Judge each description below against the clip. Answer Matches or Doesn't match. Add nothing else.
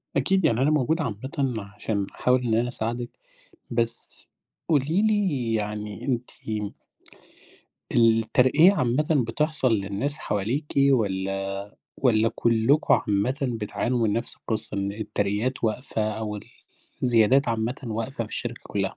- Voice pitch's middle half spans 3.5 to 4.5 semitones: Matches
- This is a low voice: Matches